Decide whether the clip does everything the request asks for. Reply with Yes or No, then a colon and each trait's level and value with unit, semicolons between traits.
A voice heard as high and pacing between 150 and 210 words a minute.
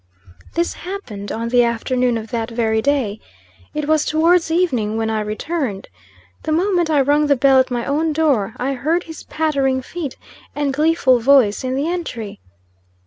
Yes: very high, 270 Hz; average, 170 wpm